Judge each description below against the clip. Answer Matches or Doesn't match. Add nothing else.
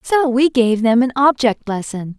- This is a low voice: Doesn't match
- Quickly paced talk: Doesn't match